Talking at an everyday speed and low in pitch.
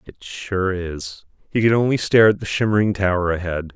Yes: average, 190 wpm; low, 100 Hz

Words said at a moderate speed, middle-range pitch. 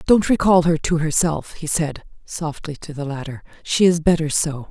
Yes: average, 190 wpm; medium, 160 Hz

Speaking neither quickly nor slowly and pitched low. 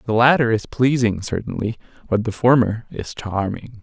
Yes: average, 155 wpm; low, 115 Hz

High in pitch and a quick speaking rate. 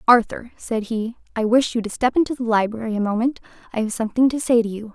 Yes: high, 230 Hz; fast, 245 wpm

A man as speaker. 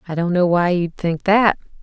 No: female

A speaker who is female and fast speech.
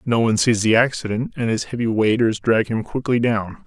No: male; fast, 215 wpm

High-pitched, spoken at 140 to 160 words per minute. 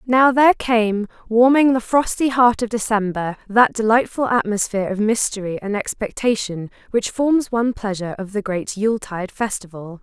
Yes: high, 220 Hz; average, 155 wpm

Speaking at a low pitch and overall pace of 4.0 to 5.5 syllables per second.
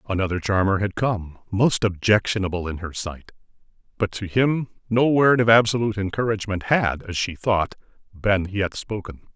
Yes: low, 100 Hz; 5.1 syllables/s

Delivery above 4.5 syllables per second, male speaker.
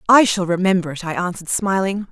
No: 6.2 syllables/s; female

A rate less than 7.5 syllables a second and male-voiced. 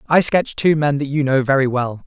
Yes: 5.1 syllables/s; male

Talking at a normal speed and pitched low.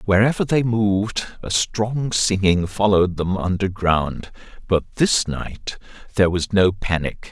No: slow, 130 wpm; low, 100 Hz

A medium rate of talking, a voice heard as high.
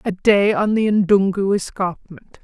Yes: average, 150 wpm; high, 195 Hz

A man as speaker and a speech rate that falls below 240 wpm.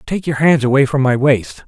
No: male; fast, 250 wpm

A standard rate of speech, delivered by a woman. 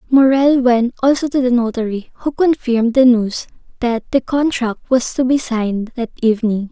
Yes: average, 170 wpm; female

